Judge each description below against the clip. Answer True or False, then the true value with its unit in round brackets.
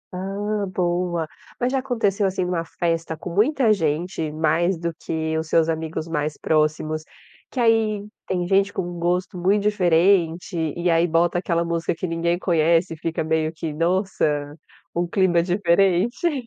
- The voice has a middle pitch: True (175 Hz)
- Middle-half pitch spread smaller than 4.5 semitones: True (3.0 semitones)